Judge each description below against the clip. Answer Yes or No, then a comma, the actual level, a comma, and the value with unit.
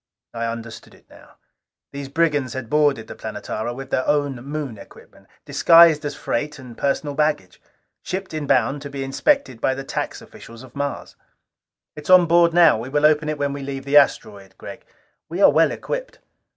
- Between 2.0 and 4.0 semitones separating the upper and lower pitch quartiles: Yes, average, 3.0 semitones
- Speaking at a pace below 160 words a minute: No, average, 190 wpm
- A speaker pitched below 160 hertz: Yes, medium, 140 Hz